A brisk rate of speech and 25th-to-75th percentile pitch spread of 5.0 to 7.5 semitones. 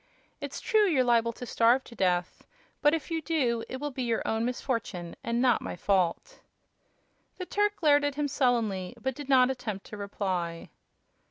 No: average, 180 wpm; wide, 5.5 semitones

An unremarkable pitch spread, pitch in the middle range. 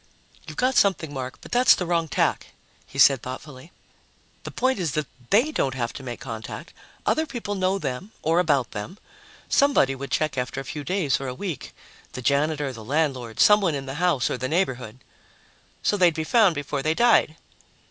No: wide, 5.9 semitones; medium, 150 Hz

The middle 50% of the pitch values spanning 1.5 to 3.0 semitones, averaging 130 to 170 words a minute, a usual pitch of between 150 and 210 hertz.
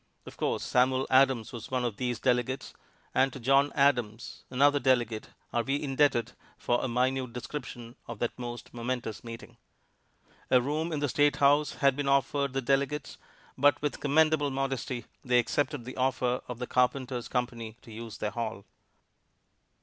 No: narrow, 2.5 semitones; average, 165 wpm; low, 130 Hz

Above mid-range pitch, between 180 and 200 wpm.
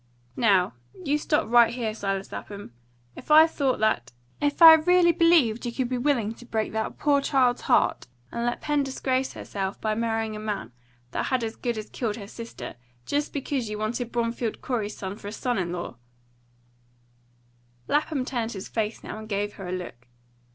Yes: high, 225 Hz; average, 190 wpm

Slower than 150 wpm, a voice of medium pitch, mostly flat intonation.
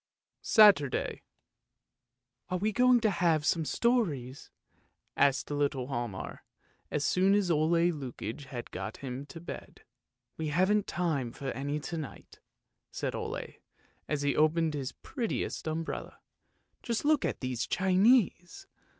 No: average, 140 wpm; medium, 155 Hz; wide, 5.5 semitones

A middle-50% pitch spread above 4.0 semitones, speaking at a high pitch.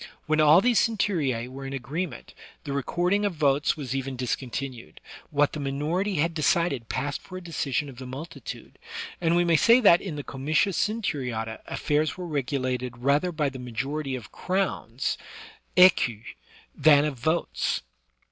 No: average, 4.6 semitones; medium, 145 Hz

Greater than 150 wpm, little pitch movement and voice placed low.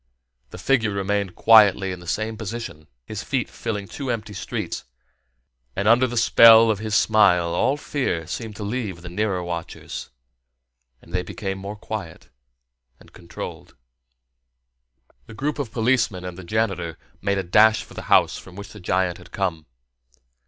No: average, 160 wpm; average, 3.6 semitones; low, 105 Hz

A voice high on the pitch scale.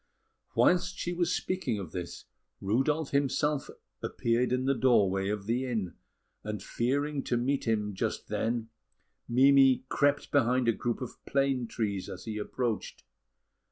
No: low, 125 Hz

